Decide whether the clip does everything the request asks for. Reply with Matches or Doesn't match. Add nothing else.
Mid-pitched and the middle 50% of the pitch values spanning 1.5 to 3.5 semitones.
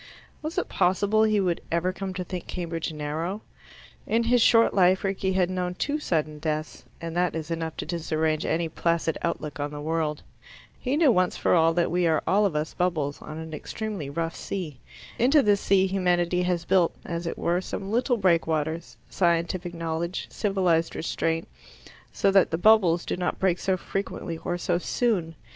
Matches